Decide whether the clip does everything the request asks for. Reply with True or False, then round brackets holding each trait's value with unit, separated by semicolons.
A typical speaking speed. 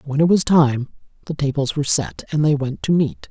False (235 wpm)